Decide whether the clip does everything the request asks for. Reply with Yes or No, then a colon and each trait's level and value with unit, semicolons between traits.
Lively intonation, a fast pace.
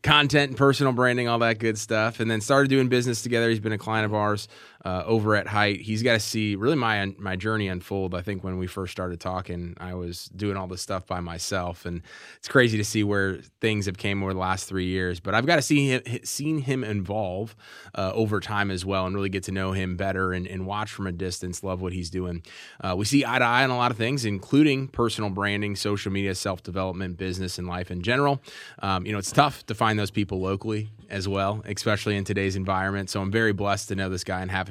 No: average, 3.0 semitones; fast, 245 wpm